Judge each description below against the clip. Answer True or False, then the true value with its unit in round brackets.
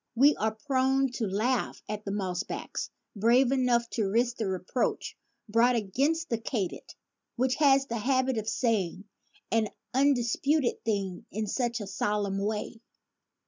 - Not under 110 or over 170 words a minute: True (150 wpm)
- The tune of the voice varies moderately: True (3.8 semitones)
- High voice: True (230 Hz)